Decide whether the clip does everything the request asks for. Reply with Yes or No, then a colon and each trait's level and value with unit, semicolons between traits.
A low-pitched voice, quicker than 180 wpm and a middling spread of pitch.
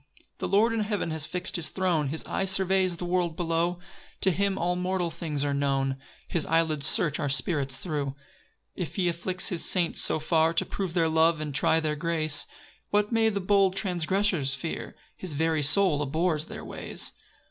No: medium, 170 Hz; average, 190 wpm; average, 3.3 semitones